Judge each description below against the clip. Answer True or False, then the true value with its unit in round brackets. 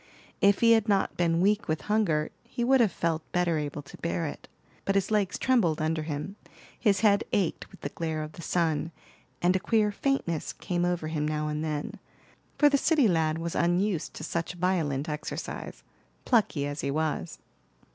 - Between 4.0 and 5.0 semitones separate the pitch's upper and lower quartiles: True (4.6 semitones)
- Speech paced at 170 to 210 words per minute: True (185 wpm)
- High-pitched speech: False (170 Hz)